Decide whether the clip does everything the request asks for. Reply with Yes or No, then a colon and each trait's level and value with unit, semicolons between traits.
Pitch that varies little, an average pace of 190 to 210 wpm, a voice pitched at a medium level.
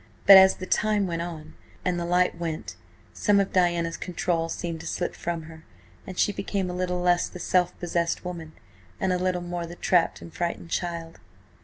Yes: narrow, 1.5 semitones; average, 195 wpm; medium, 175 Hz